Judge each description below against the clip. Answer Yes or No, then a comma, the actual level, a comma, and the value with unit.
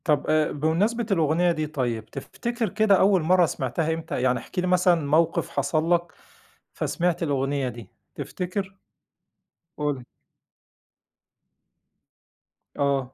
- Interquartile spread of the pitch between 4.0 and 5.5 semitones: Yes, average, 4.3 semitones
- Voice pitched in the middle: Yes, medium, 160 Hz